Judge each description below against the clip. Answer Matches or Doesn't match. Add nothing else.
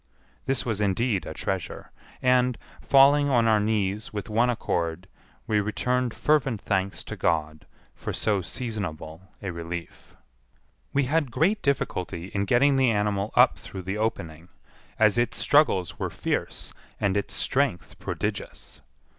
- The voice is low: Matches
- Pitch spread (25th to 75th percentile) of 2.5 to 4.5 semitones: Doesn't match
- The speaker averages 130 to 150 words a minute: Matches